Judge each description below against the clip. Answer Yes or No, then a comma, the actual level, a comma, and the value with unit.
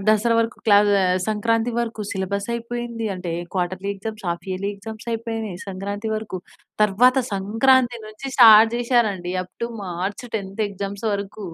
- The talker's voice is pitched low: No, high, 215 Hz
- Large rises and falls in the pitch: No, average, 2.8 semitones